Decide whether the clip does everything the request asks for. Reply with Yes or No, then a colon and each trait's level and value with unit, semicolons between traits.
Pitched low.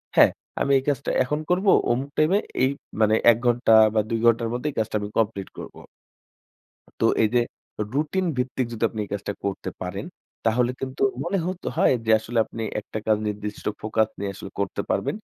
Yes: low, 115 Hz